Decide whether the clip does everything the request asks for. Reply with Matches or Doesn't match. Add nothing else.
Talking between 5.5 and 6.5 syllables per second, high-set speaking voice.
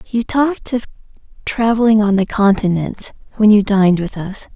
Doesn't match